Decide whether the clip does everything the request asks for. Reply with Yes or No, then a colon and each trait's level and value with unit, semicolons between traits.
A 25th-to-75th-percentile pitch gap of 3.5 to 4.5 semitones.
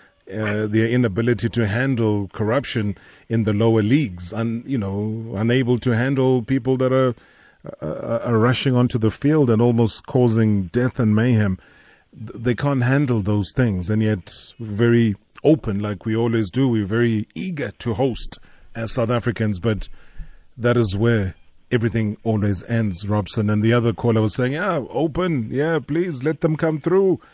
No: average, 3.0 semitones